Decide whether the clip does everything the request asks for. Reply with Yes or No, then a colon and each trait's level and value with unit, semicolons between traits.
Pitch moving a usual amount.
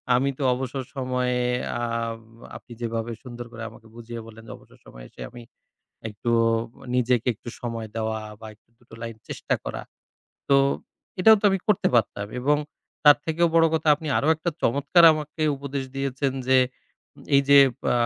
Yes: average, 3.5 semitones